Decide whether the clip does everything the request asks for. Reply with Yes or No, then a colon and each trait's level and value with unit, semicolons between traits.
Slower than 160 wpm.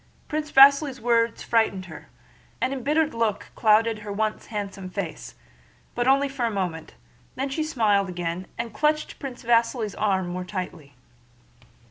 Yes: average, 145 wpm